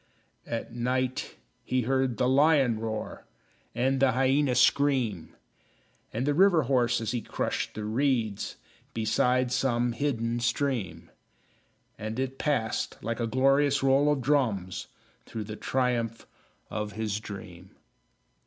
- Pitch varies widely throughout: No, average, 3.3 semitones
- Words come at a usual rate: No, slow, 125 wpm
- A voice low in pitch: Yes, low, 125 Hz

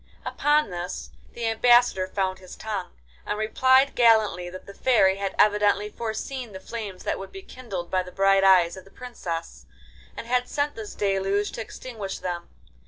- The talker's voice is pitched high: Yes, high, 205 Hz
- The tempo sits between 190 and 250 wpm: No, average, 170 wpm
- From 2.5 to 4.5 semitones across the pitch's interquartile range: Yes, average, 3.9 semitones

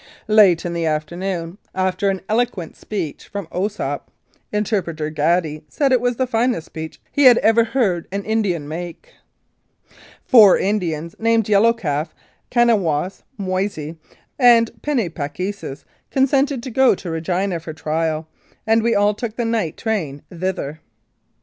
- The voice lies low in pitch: No, high, 195 Hz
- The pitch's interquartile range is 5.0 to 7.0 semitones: Yes, wide, 5.6 semitones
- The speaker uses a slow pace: No, average, 145 wpm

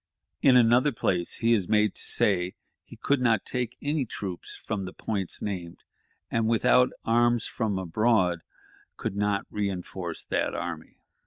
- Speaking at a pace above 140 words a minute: Yes, average, 150 wpm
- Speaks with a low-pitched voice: Yes, low, 105 Hz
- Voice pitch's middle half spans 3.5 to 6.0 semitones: Yes, average, 4.1 semitones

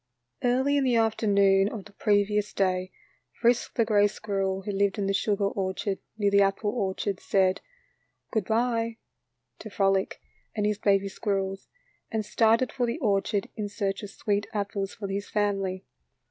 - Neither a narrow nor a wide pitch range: No, narrow, 2.0 semitones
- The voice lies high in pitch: Yes, high, 205 Hz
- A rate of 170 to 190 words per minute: No, average, 160 wpm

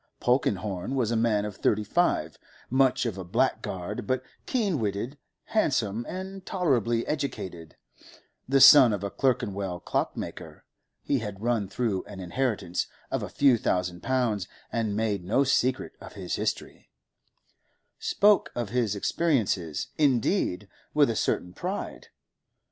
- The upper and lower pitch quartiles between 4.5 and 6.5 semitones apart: Yes, average, 5.1 semitones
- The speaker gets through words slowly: Yes, slow, 130 wpm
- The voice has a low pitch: Yes, low, 115 Hz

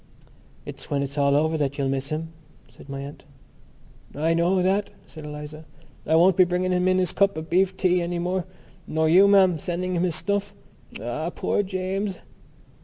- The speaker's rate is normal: Yes, average, 185 wpm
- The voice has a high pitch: No, medium, 175 Hz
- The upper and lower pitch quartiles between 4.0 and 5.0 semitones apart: No, average, 3.4 semitones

